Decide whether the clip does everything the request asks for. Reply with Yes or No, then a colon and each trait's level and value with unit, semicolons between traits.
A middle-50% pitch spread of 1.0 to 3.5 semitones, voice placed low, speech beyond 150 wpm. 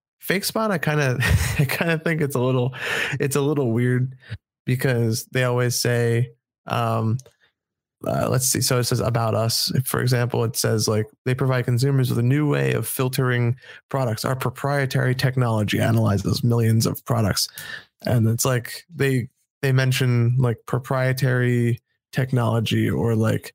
Yes: narrow, 2.5 semitones; low, 125 Hz; average, 160 wpm